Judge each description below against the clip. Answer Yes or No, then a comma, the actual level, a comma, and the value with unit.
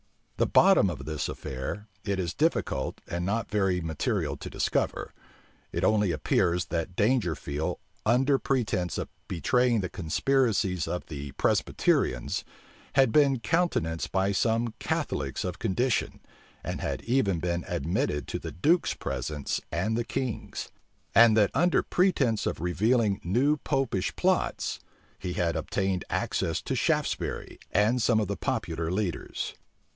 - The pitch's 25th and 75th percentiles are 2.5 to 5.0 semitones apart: No, wide, 5.6 semitones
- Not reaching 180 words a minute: Yes, average, 140 wpm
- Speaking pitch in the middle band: No, low, 100 Hz